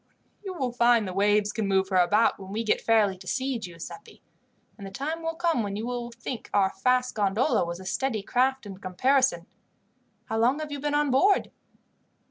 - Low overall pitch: No, high, 230 Hz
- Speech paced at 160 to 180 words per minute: No, average, 200 wpm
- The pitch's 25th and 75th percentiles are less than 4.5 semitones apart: No, average, 5.2 semitones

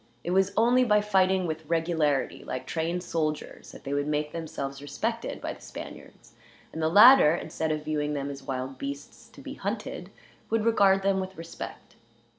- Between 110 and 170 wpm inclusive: No, average, 180 wpm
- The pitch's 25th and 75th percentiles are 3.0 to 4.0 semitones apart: No, average, 4.6 semitones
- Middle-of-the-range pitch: Yes, medium, 160 Hz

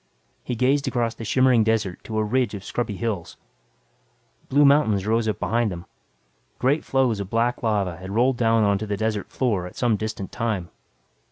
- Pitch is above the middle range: No, low, 110 Hz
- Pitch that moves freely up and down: No, average, 3.2 semitones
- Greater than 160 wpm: Yes, average, 180 wpm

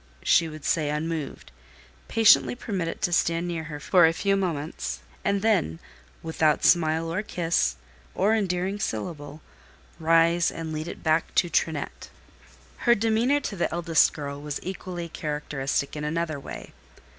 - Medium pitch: Yes, medium, 165 Hz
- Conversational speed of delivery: Yes, average, 145 wpm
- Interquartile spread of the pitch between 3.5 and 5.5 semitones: No, average, 3.1 semitones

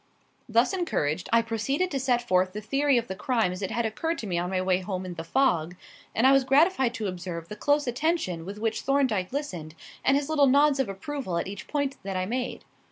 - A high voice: Yes, high, 230 Hz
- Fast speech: Yes, fast, 230 wpm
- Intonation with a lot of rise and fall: Yes, wide, 6.8 semitones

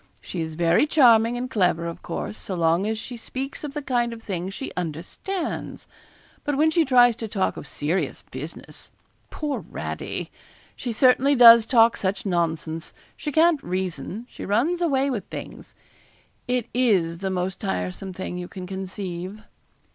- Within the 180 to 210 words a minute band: No, average, 160 wpm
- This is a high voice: Yes, high, 215 Hz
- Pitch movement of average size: No, wide, 6.1 semitones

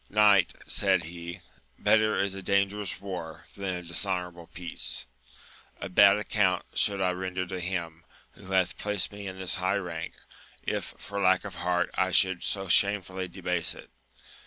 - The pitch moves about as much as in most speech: No, narrow, 1.9 semitones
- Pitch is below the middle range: Yes, very low, 95 Hz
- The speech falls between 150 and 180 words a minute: Yes, average, 160 wpm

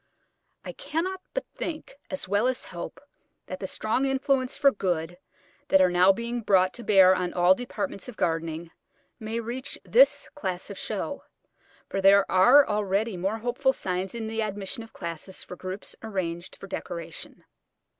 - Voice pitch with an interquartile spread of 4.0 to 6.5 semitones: Yes, average, 4.8 semitones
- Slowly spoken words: No, average, 165 wpm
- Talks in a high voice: Yes, high, 200 Hz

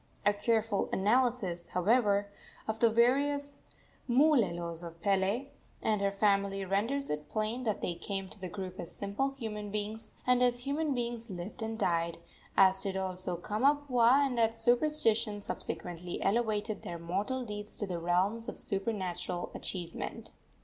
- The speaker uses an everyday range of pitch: Yes, average, 4.1 semitones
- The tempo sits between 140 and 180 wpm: Yes, average, 150 wpm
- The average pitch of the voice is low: No, high, 210 Hz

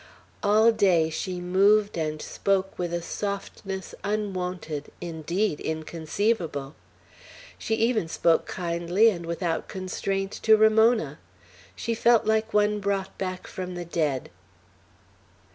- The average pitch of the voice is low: No, medium, 185 Hz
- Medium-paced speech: No, slow, 115 wpm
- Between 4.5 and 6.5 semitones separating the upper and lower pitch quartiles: No, average, 3.8 semitones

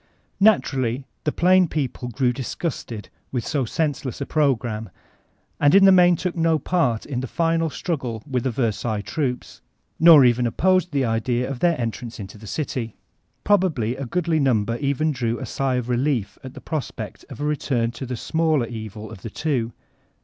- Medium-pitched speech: No, low, 130 Hz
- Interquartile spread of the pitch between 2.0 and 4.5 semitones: No, average, 5.2 semitones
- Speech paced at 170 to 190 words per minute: Yes, average, 185 wpm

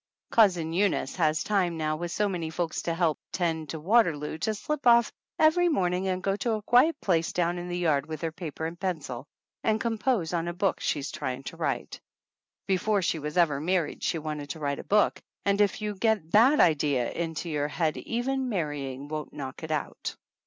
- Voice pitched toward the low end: No, medium, 170 Hz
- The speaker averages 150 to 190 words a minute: No, fast, 205 wpm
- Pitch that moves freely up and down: No, average, 4.9 semitones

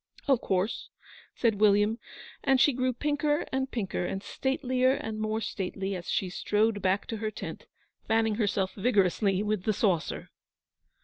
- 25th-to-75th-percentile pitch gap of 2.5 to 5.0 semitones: Yes, average, 4.4 semitones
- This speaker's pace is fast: No, average, 150 wpm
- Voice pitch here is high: Yes, high, 215 Hz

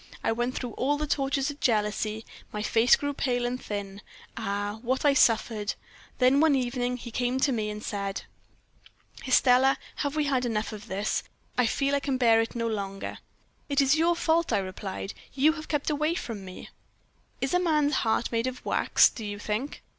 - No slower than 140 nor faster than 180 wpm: No, average, 190 wpm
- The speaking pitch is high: Yes, high, 245 Hz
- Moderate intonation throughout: Yes, average, 4.7 semitones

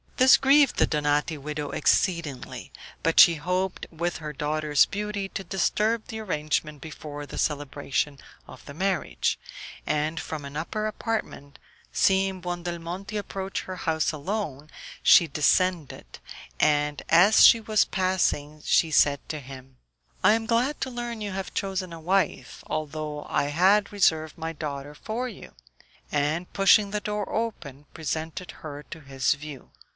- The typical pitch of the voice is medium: Yes, medium, 165 Hz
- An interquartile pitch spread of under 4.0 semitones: No, average, 4.9 semitones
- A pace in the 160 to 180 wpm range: No, average, 145 wpm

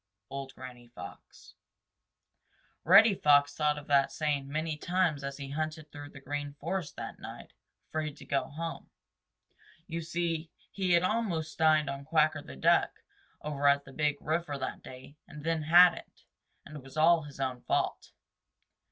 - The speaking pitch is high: No, medium, 150 Hz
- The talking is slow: No, average, 160 wpm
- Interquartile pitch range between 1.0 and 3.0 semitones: Yes, average, 2.7 semitones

